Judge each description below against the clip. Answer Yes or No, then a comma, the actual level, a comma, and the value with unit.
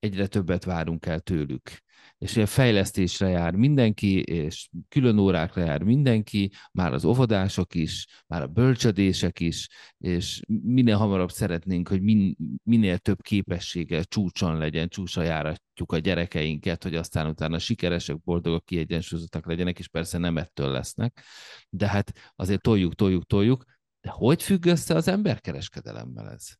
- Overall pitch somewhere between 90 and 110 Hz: Yes, very low, 95 Hz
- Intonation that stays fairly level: No, average, 4.4 semitones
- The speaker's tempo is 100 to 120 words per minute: No, average, 140 wpm